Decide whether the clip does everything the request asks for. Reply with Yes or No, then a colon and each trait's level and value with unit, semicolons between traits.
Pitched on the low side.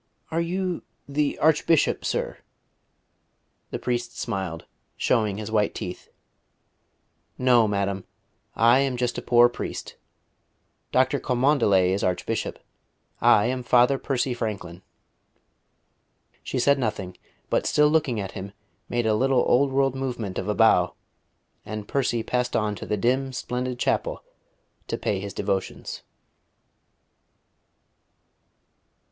Yes: low, 120 Hz